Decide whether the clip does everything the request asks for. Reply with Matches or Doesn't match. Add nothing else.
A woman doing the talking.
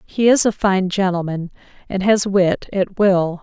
Matches